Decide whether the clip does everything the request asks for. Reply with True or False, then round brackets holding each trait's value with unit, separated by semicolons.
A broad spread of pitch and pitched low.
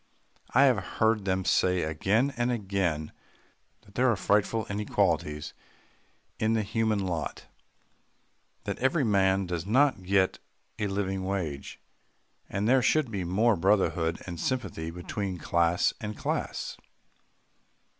False (3.8 semitones; 100 Hz)